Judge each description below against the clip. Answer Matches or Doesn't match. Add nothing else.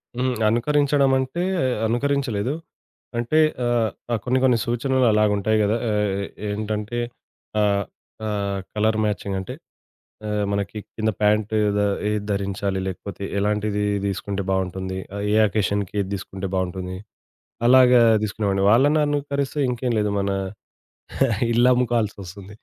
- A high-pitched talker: Doesn't match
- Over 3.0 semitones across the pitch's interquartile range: Matches